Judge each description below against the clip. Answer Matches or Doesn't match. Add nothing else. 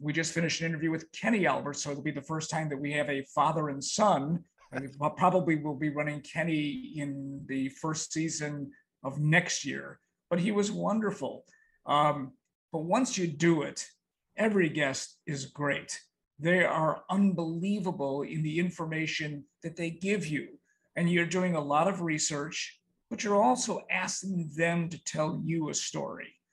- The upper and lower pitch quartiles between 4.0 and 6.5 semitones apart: Doesn't match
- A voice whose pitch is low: Doesn't match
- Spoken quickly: Doesn't match